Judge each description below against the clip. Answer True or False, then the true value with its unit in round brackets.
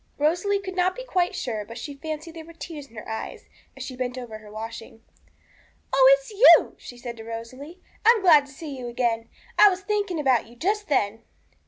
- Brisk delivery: True (215 wpm)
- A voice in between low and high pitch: False (280 Hz)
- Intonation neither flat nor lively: False (7.3 semitones)